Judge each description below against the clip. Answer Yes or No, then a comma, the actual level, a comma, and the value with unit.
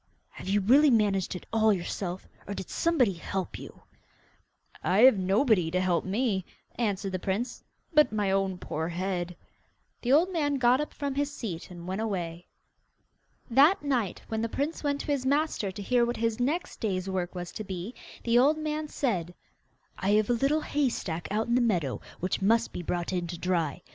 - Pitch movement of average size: No, wide, 6.1 semitones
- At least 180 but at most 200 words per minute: Yes, average, 195 wpm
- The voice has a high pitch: Yes, high, 210 Hz